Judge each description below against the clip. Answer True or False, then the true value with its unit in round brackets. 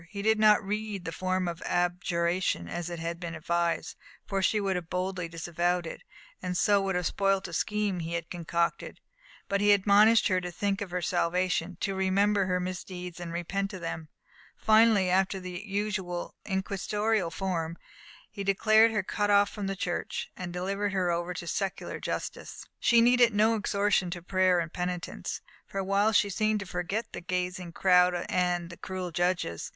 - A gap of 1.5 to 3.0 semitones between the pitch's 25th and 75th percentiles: True (2.5 semitones)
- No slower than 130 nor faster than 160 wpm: False (175 wpm)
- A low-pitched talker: False (185 Hz)